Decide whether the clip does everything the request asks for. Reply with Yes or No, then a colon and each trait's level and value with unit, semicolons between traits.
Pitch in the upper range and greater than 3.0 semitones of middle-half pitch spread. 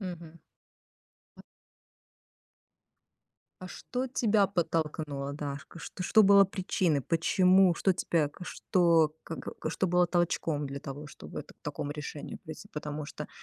No: medium, 165 Hz; average, 3.8 semitones